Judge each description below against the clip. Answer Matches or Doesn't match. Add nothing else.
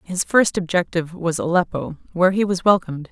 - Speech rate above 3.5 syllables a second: Matches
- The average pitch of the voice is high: Doesn't match